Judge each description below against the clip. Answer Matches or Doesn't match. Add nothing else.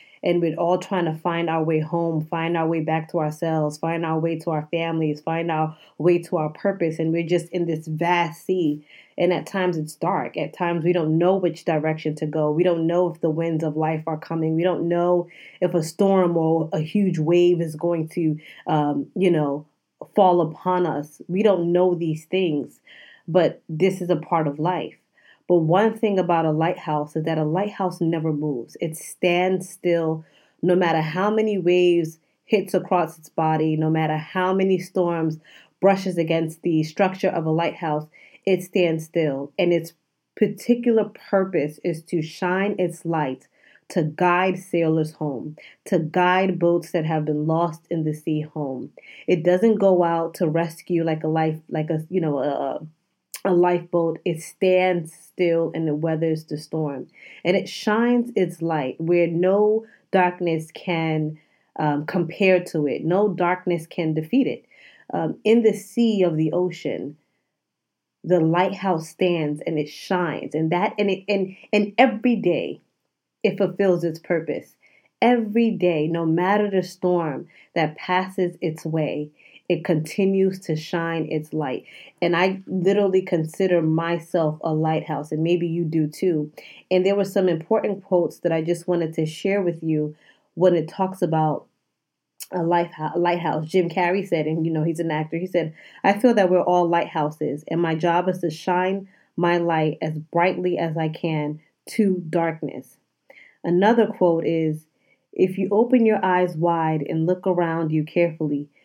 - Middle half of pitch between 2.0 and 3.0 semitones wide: Matches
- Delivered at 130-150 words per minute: Doesn't match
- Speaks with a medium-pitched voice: Matches